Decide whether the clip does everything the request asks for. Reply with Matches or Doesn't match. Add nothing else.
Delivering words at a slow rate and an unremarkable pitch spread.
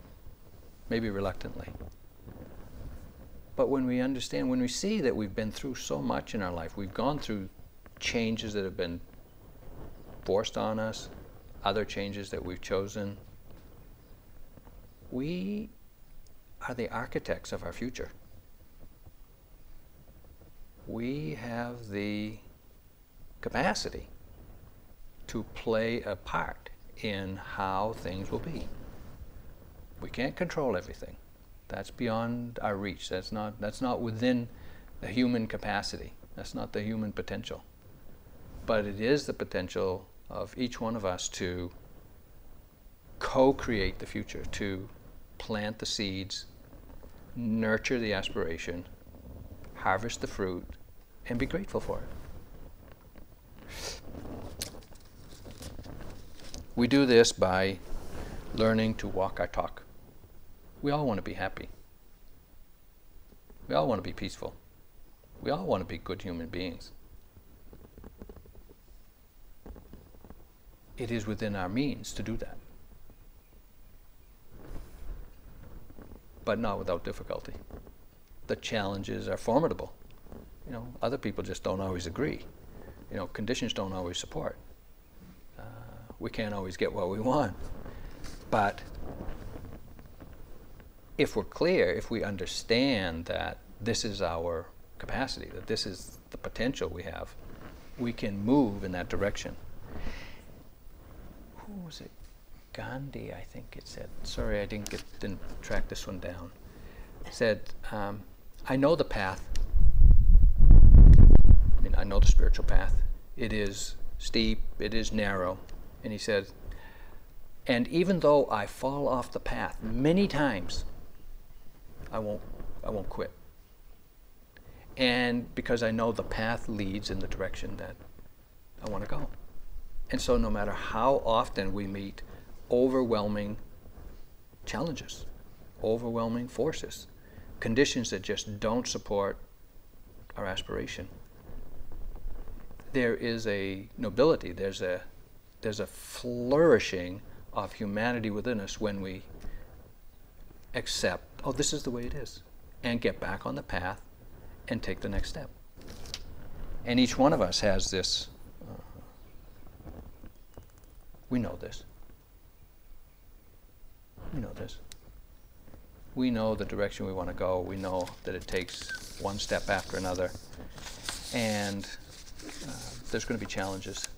Matches